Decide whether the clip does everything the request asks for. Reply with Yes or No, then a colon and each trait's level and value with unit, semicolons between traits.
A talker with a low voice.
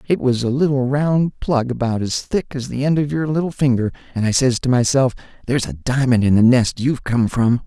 Yes: low, 130 Hz